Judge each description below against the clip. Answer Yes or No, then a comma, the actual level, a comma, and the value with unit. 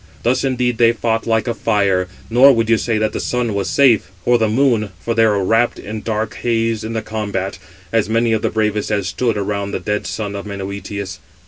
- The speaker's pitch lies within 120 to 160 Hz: No, low, 110 Hz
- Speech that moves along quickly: Yes, fast, 220 wpm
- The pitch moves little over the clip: Yes, narrow, 2.2 semitones